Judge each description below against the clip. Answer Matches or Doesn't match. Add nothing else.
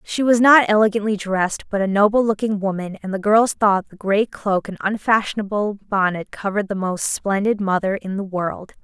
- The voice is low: Doesn't match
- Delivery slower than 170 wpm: Doesn't match